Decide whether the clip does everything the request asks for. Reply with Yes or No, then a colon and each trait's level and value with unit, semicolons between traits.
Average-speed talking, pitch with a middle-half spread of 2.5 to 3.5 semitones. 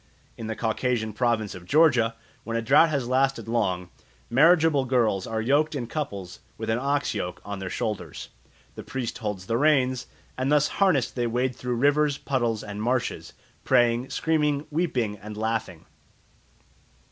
No: average, 160 wpm; average, 4.2 semitones